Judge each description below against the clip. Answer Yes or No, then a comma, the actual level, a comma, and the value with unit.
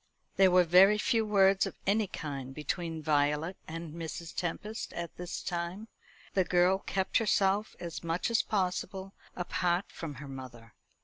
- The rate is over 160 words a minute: No, average, 150 wpm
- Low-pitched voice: No, medium, 175 Hz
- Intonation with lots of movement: No, average, 3.2 semitones